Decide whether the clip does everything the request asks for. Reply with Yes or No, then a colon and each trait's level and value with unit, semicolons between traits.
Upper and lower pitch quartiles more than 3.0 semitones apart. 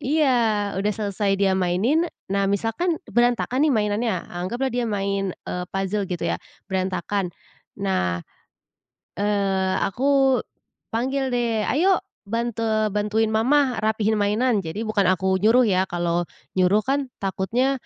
Yes: average, 4.0 semitones